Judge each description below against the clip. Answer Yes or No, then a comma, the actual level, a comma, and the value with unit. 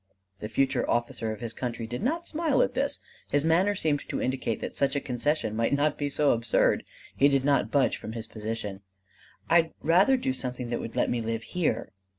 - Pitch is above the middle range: No, low, 130 Hz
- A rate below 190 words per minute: No, fast, 205 wpm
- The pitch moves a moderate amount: Yes, average, 5.0 semitones